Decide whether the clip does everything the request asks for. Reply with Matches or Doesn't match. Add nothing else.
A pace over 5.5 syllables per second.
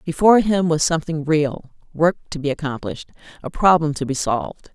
Matches